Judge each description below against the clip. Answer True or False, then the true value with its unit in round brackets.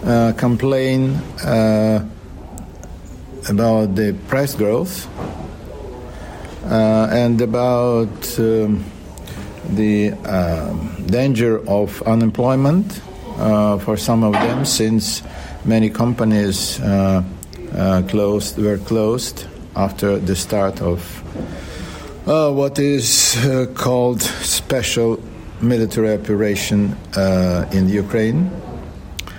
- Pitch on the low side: True (105 Hz)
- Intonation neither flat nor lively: True (3.7 semitones)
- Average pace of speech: False (90 wpm)